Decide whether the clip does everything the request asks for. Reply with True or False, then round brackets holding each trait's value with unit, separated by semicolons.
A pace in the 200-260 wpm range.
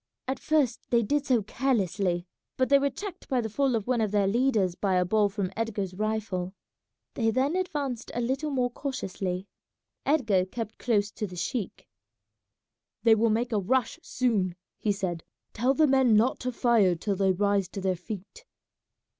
False (180 wpm)